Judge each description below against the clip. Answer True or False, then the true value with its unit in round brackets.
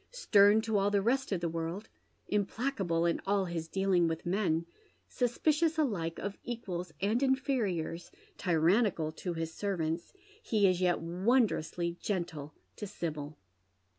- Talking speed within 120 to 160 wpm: True (140 wpm)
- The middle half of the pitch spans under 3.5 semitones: False (4.6 semitones)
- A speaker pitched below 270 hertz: True (190 Hz)